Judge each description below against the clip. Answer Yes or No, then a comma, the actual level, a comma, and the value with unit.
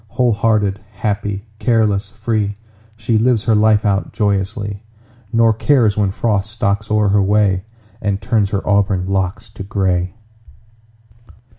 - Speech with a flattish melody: Yes, narrow, 2.0 semitones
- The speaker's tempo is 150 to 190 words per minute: No, slow, 135 wpm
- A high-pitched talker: No, low, 105 Hz